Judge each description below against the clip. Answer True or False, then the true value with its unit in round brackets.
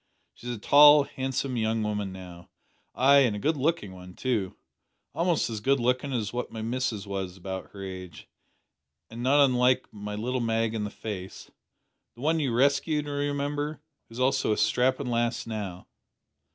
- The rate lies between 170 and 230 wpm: True (175 wpm)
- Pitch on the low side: True (120 Hz)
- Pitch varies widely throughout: False (4.9 semitones)